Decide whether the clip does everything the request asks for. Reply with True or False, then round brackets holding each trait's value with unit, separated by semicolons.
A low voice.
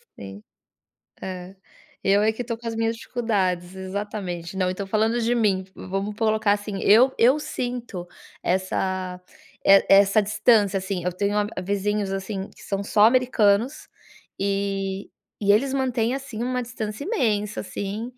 False (205 Hz)